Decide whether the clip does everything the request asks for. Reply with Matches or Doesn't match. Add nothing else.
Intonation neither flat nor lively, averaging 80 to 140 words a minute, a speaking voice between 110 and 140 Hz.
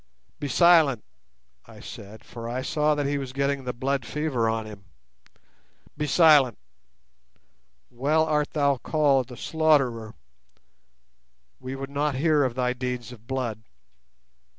Matches